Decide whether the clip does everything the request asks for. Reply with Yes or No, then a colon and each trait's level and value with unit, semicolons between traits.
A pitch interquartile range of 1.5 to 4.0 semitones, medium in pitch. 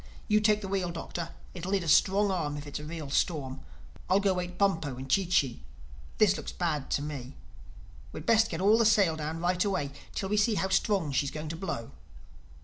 No: average, 4.7 semitones; medium, 175 Hz